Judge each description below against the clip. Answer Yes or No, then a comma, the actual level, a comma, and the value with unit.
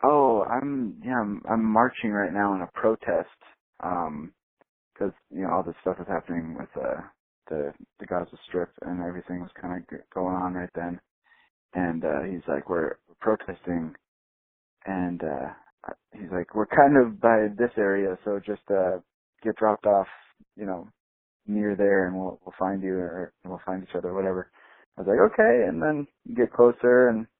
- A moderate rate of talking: Yes, average, 180 wpm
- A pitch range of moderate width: Yes, average, 3.6 semitones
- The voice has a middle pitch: No, very low, 95 Hz